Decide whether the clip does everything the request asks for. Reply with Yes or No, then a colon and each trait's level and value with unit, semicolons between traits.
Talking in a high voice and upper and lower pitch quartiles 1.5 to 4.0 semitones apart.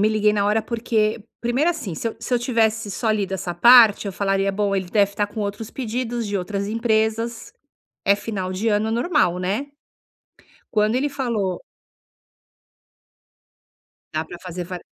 Yes: high, 215 Hz; average, 2.8 semitones